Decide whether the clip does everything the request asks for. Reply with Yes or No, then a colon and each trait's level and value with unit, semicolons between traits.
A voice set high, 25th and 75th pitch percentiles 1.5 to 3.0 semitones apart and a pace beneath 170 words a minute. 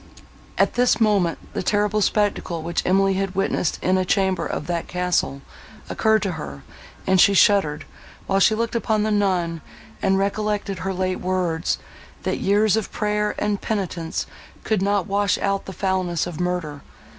Yes: high, 195 Hz; average, 2.7 semitones; average, 155 wpm